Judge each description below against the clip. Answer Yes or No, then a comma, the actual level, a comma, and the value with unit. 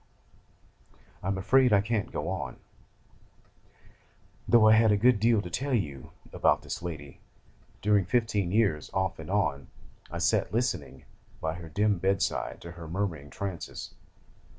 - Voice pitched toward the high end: No, low, 100 Hz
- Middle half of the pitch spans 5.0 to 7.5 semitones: No, average, 4.6 semitones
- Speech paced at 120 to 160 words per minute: Yes, average, 150 wpm